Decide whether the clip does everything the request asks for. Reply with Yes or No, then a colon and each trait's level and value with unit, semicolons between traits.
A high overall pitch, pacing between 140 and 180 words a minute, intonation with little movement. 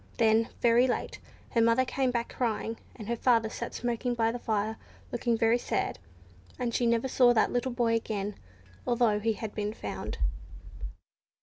Yes: high, 230 Hz; average, 170 wpm; narrow, 1.6 semitones